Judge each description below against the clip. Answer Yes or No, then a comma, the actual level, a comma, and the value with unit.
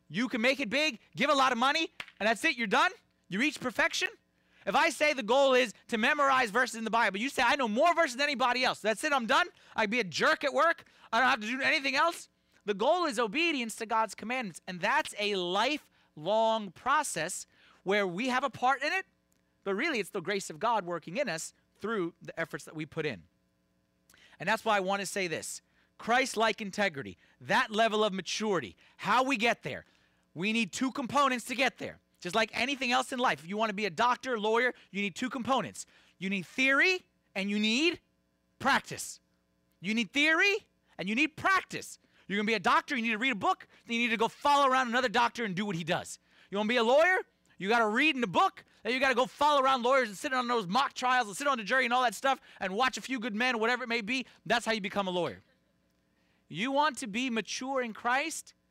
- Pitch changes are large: No, average, 4.8 semitones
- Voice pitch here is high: Yes, high, 240 Hz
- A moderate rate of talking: No, fast, 235 wpm